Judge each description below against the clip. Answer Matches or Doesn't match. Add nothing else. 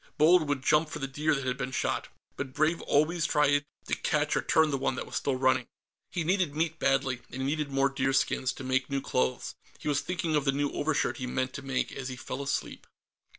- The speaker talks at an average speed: Doesn't match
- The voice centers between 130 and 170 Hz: Matches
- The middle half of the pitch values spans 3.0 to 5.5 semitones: Doesn't match